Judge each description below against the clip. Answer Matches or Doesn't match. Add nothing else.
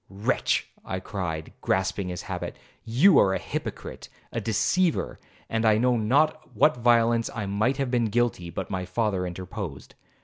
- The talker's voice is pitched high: Doesn't match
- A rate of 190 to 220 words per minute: Doesn't match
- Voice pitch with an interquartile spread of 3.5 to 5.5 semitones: Matches